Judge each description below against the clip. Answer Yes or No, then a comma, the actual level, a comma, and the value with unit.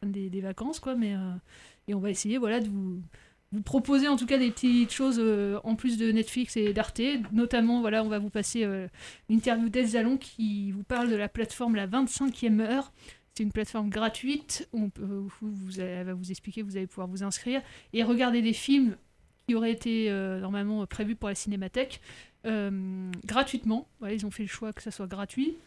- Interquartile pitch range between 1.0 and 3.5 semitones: Yes, average, 3.1 semitones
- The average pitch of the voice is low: No, high, 220 Hz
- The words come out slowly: No, average, 205 wpm